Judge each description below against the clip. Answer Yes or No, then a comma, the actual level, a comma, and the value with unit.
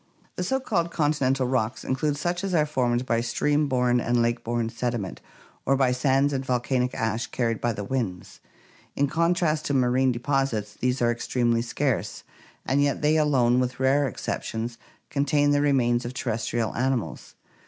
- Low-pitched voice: Yes, low, 130 Hz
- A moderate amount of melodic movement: Yes, average, 3.2 semitones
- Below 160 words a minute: No, average, 165 wpm